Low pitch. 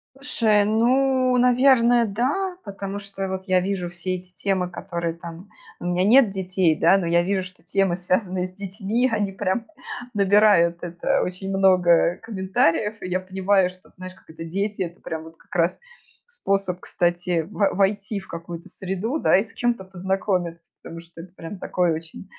No: high, 190 Hz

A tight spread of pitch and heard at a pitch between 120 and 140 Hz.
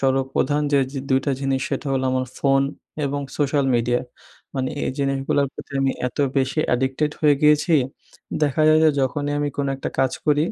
Yes: narrow, 1.7 semitones; low, 135 Hz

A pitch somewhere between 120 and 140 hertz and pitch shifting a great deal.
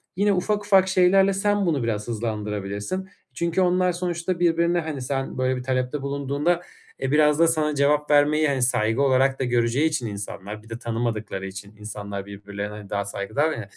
Yes: low, 135 Hz; wide, 7.7 semitones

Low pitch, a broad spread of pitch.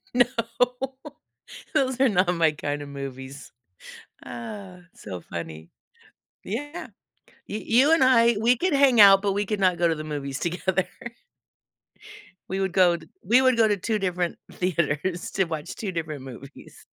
No: medium, 185 Hz; wide, 6.9 semitones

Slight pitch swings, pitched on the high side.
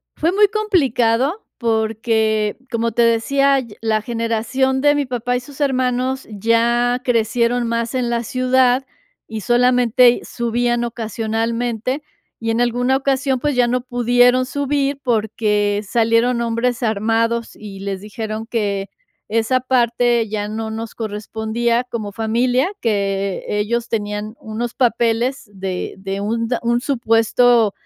Yes: narrow, 2.2 semitones; high, 235 Hz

